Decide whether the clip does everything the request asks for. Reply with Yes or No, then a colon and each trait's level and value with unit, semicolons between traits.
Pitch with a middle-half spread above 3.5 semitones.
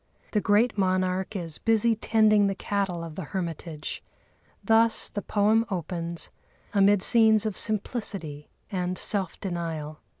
Yes: average, 3.9 semitones